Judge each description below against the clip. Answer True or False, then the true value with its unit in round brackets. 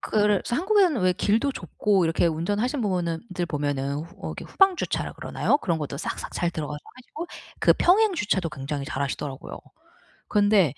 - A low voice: False (185 Hz)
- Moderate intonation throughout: False (7.9 semitones)